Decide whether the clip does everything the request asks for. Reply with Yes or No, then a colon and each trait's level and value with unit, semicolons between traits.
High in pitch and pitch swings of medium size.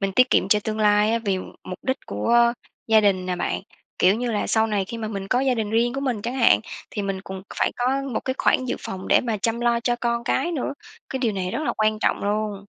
Yes: high, 220 Hz; average, 3.3 semitones